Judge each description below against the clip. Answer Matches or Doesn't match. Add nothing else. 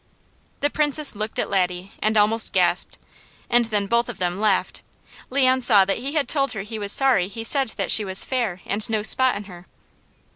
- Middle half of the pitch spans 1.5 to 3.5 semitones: Doesn't match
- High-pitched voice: Matches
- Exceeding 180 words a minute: Matches